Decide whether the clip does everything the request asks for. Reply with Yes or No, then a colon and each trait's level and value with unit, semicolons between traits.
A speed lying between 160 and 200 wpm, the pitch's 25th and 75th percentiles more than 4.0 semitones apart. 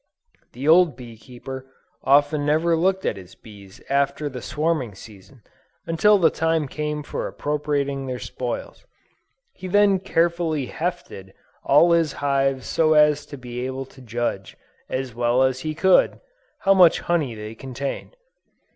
No: average, 145 wpm; average, 4.5 semitones